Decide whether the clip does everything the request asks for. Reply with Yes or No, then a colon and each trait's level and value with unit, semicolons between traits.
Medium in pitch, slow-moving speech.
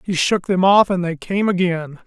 No: medium, 180 Hz; fast, 205 wpm